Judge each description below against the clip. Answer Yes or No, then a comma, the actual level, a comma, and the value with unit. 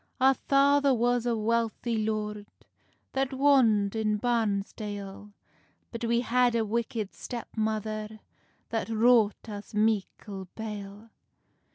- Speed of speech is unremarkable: No, slow, 110 wpm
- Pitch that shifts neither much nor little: No, narrow, 2.3 semitones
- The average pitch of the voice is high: Yes, high, 220 Hz